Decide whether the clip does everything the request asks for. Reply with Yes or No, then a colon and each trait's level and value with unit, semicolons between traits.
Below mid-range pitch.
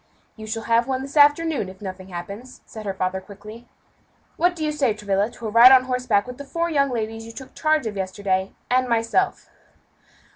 No: high, 230 Hz